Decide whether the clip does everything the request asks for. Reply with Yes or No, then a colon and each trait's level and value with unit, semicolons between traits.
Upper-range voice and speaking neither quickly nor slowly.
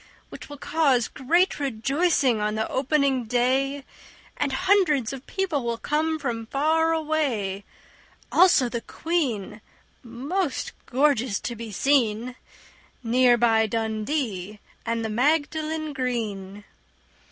No: very high, 255 Hz; slow, 115 wpm